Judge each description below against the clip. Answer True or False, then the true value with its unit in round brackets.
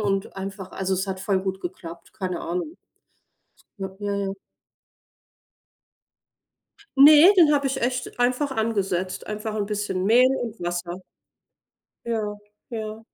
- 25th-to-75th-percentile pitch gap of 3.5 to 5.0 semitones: True (4.1 semitones)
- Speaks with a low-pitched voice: False (205 Hz)